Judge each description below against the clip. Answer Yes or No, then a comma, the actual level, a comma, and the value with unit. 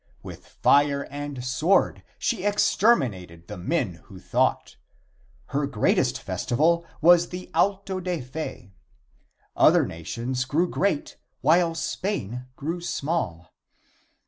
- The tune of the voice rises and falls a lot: Yes, wide, 6.2 semitones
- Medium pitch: Yes, medium, 145 Hz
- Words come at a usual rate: No, slow, 110 wpm